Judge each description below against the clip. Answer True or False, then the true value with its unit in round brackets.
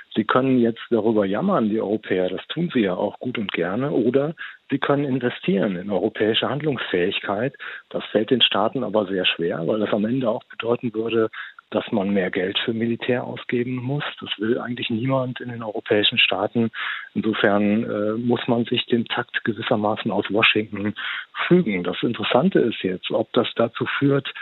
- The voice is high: False (120 Hz)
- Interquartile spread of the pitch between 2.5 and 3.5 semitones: True (2.8 semitones)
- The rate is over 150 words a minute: True (175 wpm)